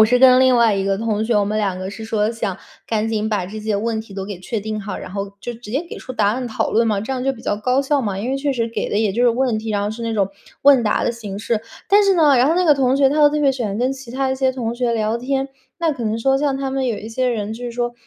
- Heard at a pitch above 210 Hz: Yes, high, 230 Hz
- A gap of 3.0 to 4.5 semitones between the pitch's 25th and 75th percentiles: Yes, average, 3.7 semitones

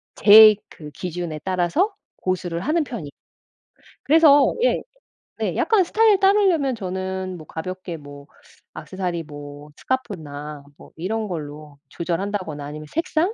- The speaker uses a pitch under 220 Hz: Yes, medium, 185 Hz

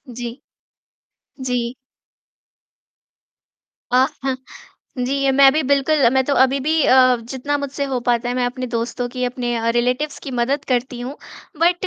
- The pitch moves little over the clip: Yes, narrow, 2.3 semitones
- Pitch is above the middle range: Yes, very high, 260 Hz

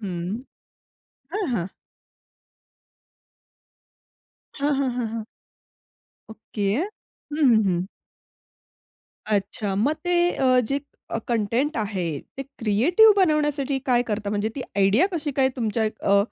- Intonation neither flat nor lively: No, wide, 5.8 semitones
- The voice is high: Yes, high, 240 Hz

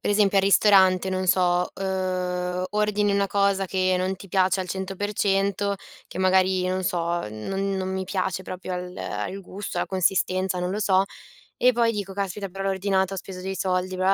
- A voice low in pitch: No, high, 190 Hz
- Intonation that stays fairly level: Yes, narrow, 1.2 semitones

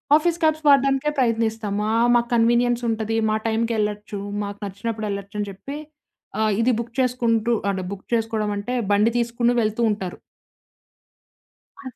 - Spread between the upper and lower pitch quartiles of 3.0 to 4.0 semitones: No, narrow, 2.4 semitones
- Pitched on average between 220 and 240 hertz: Yes, high, 225 Hz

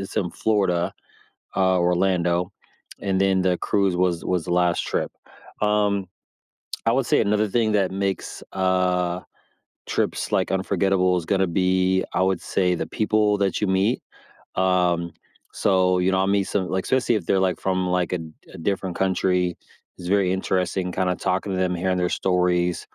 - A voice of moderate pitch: No, very low, 95 Hz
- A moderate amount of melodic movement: No, narrow, 1.4 semitones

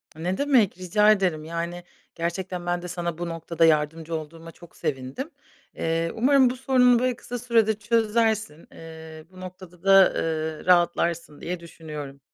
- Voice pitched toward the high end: No, medium, 175 Hz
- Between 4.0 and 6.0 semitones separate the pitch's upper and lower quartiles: Yes, average, 4.7 semitones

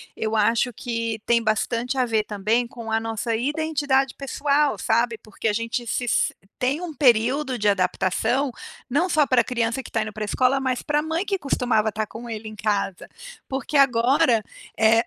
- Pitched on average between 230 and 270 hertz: Yes, high, 235 Hz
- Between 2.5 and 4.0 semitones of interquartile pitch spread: Yes, average, 3.5 semitones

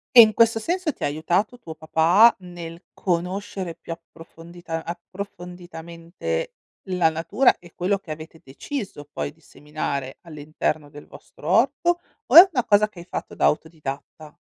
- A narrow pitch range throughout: No, average, 4.6 semitones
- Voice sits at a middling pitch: Yes, medium, 175 Hz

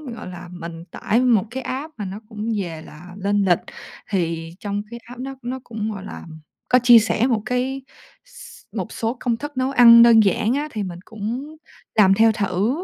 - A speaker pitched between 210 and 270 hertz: Yes, high, 220 Hz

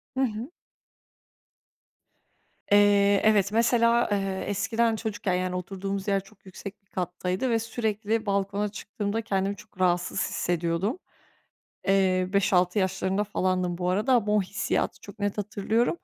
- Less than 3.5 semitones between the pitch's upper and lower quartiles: Yes, narrow, 2.5 semitones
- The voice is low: No, high, 200 Hz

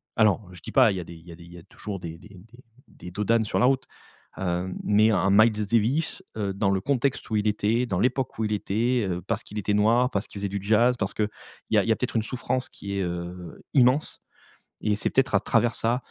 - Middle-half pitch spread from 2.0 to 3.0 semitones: No, average, 3.5 semitones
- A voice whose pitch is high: No, low, 105 Hz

